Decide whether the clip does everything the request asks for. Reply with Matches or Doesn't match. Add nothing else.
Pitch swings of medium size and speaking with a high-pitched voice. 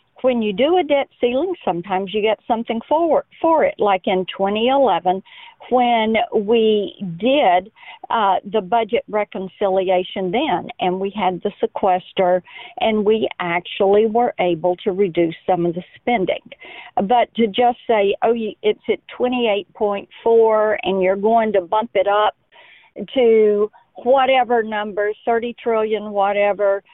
Matches